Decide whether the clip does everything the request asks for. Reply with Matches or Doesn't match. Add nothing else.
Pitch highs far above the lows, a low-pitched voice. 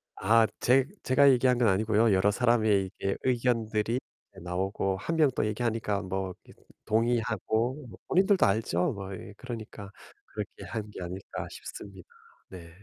Doesn't match